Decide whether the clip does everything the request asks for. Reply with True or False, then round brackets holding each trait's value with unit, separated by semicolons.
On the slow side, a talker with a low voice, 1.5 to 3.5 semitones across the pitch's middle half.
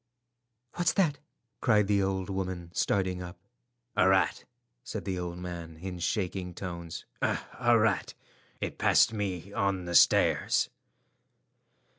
True (120 wpm; 95 Hz; 2.5 semitones)